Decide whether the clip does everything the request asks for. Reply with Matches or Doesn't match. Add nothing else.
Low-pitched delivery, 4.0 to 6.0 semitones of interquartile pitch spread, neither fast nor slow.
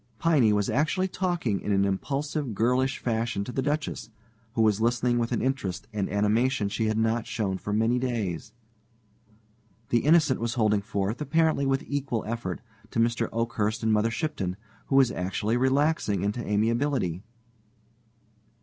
Matches